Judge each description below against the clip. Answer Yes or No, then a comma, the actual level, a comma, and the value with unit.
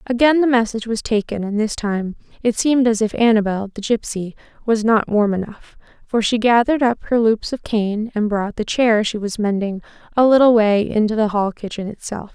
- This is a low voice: No, high, 220 Hz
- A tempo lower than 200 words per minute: No, fast, 205 wpm